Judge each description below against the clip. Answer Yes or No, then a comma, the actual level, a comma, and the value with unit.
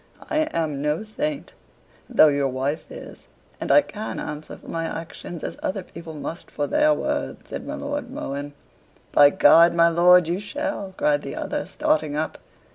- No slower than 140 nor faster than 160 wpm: No, average, 175 wpm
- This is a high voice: No, medium, 170 Hz